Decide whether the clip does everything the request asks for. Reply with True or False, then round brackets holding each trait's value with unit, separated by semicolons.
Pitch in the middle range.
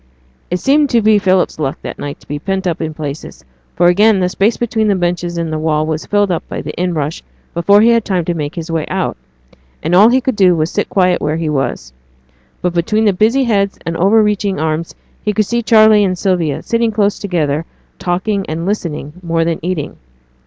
True (180 Hz)